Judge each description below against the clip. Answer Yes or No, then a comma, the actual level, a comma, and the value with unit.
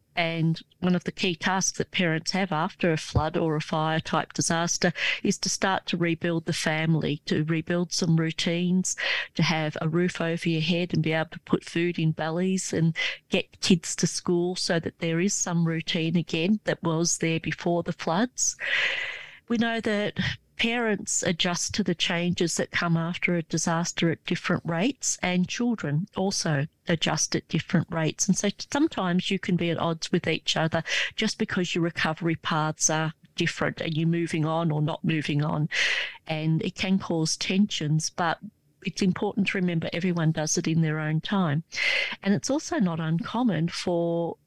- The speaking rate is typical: Yes, average, 180 wpm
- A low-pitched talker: No, medium, 170 Hz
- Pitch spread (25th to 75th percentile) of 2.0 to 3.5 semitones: Yes, narrow, 2.4 semitones